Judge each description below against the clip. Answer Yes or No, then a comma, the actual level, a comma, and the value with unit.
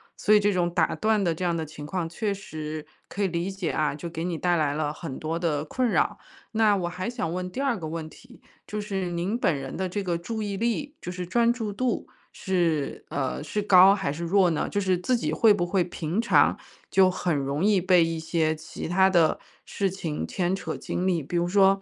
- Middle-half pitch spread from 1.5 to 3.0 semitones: No, average, 3.6 semitones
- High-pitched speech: No, medium, 180 Hz